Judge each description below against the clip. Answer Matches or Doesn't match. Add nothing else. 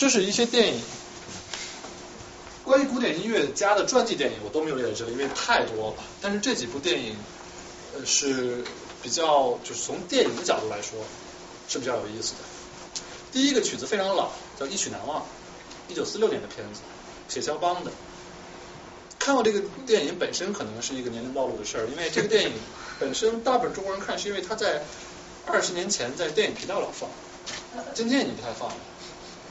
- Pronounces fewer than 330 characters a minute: Matches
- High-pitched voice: Matches